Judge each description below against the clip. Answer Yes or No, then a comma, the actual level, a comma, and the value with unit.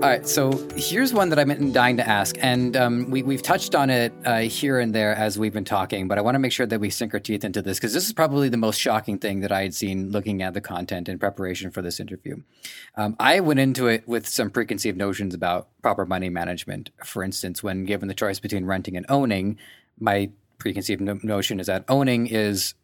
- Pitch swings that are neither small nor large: Yes, average, 4.3 semitones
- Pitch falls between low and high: No, low, 105 Hz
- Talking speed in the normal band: No, fast, 235 wpm